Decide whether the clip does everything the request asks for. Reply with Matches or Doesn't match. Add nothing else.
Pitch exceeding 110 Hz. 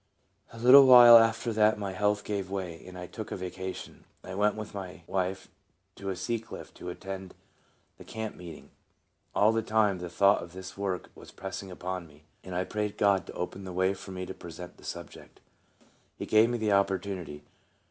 Doesn't match